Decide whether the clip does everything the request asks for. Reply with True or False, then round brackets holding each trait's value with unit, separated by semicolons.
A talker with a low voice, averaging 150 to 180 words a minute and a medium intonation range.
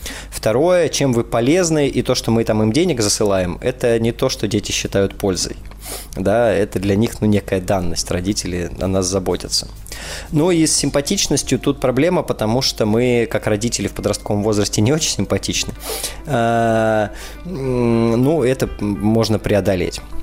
True (115 Hz; 155 wpm; 4.2 semitones)